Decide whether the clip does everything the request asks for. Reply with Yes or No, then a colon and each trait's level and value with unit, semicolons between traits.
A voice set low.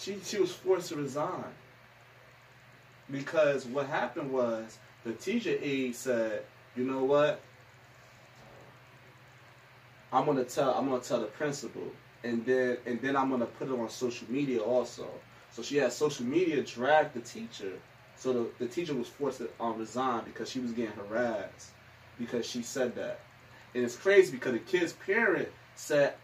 Yes: low, 130 Hz